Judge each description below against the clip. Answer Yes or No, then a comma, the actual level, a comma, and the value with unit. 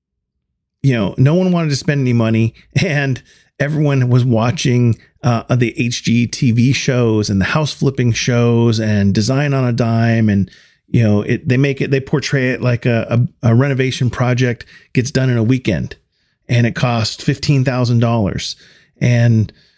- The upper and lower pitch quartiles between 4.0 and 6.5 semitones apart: No, narrow, 2.6 semitones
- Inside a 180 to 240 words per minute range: No, average, 160 wpm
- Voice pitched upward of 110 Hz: Yes, low, 120 Hz